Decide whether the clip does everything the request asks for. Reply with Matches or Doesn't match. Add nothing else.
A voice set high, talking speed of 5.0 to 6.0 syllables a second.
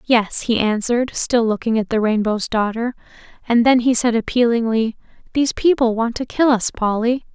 Matches